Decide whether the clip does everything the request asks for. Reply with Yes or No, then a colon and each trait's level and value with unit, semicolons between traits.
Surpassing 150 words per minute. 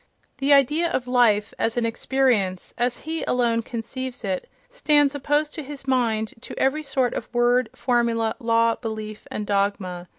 Yes: average, 160 wpm